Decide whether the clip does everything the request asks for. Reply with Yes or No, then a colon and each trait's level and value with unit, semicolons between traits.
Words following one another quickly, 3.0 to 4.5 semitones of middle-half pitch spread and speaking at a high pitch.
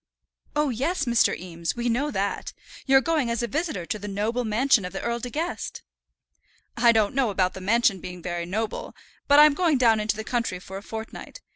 No: fast, 210 wpm; average, 5.2 semitones; high, 230 Hz